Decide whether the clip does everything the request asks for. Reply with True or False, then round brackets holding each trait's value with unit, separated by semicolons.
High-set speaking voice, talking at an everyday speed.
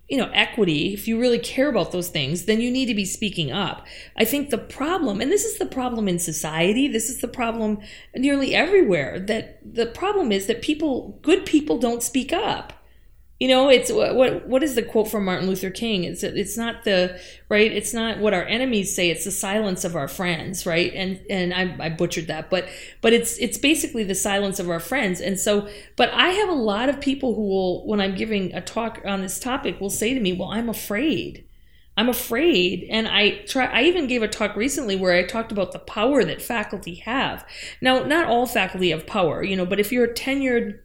False (220 Hz; 220 wpm)